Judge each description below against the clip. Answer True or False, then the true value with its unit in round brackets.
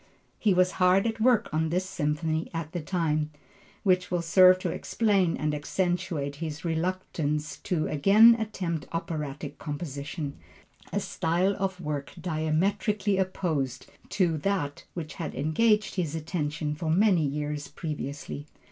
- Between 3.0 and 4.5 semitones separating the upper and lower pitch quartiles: True (3.8 semitones)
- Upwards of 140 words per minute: False (135 wpm)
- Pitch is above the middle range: False (165 Hz)